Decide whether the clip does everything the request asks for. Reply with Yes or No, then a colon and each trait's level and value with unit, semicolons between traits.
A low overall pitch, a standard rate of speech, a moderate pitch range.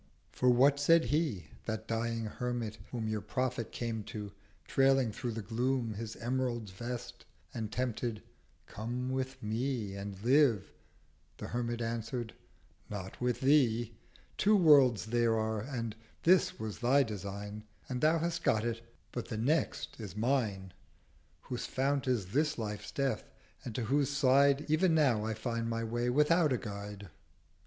Yes: low, 120 Hz; average, 150 wpm; average, 3.5 semitones